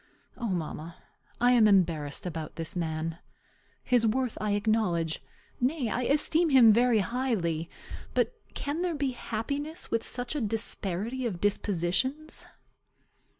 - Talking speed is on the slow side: Yes, slow, 130 wpm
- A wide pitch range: Yes, wide, 6.8 semitones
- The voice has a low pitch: No, high, 225 Hz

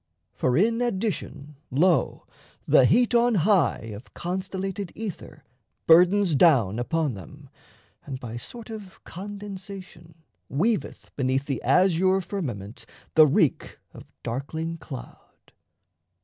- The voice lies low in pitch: No, medium, 170 Hz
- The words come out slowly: Yes, slow, 110 wpm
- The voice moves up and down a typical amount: No, wide, 6.5 semitones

